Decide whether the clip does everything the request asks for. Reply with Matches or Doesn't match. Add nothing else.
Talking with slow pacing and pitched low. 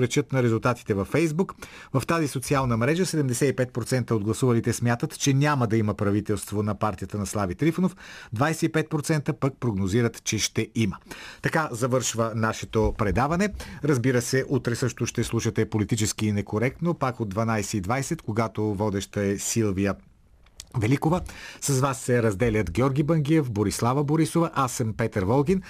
Doesn't match